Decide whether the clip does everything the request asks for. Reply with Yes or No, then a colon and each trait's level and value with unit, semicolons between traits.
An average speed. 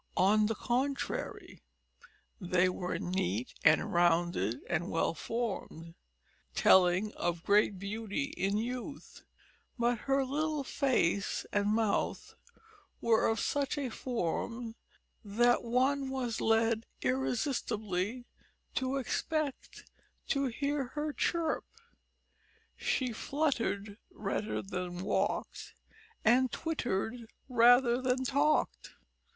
No: slow, 100 wpm